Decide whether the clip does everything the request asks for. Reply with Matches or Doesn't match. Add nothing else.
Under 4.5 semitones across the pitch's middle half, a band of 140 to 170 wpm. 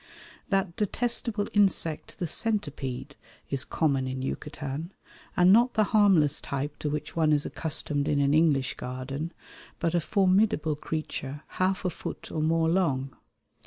Doesn't match